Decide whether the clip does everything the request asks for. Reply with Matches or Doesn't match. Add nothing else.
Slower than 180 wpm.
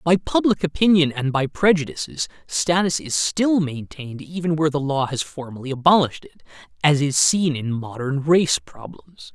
Matches